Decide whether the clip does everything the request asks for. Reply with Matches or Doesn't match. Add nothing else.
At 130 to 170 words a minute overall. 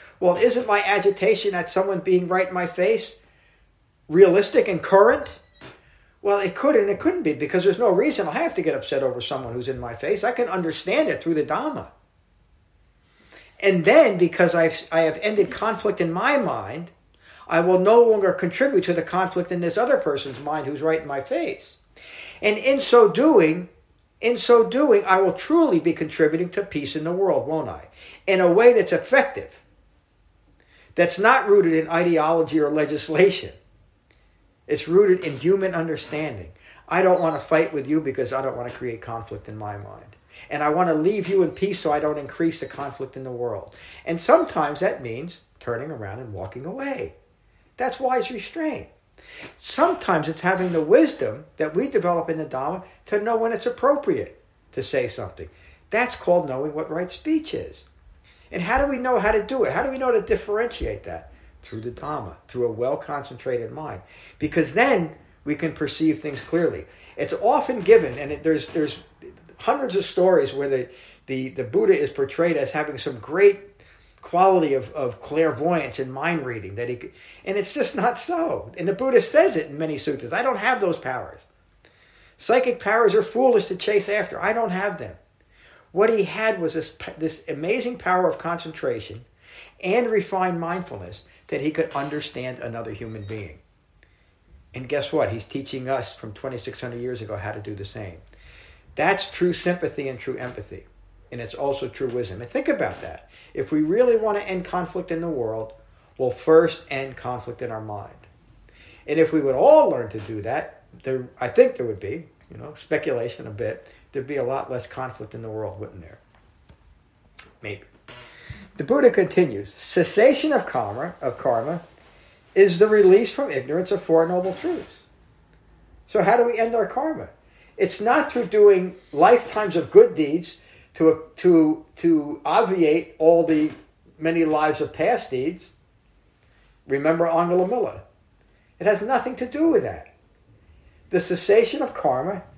Doesn't match